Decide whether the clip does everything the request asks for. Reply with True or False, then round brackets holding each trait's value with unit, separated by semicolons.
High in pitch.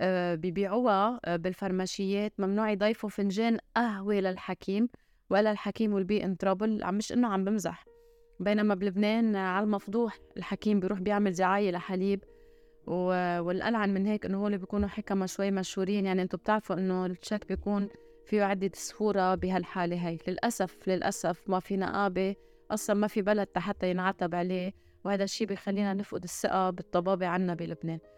True (195 Hz)